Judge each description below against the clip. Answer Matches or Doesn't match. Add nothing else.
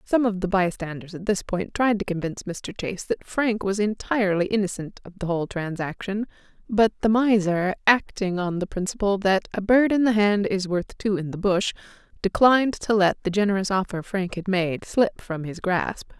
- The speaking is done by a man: Doesn't match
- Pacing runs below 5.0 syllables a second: Doesn't match